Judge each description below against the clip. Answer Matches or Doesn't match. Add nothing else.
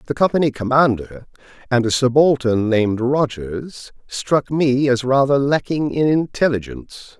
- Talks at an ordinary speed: Doesn't match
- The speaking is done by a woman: Doesn't match